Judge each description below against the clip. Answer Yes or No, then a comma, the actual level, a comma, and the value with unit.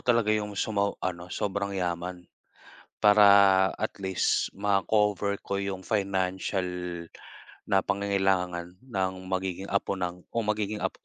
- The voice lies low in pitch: Yes, low, 100 Hz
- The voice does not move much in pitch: Yes, narrow, 1.6 semitones